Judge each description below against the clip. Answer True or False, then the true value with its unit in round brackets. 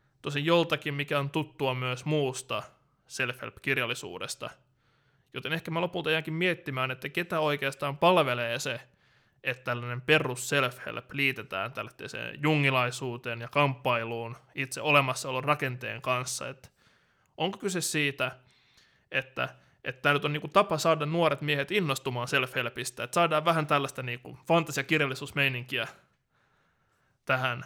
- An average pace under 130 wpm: True (120 wpm)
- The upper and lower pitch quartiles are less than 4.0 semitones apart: True (3.3 semitones)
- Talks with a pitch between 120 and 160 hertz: True (140 Hz)